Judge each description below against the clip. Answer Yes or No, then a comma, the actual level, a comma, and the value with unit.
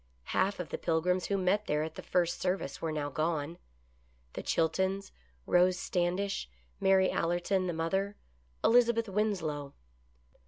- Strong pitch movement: No, average, 3.1 semitones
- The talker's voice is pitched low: No, medium, 180 Hz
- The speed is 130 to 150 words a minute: Yes, slow, 135 wpm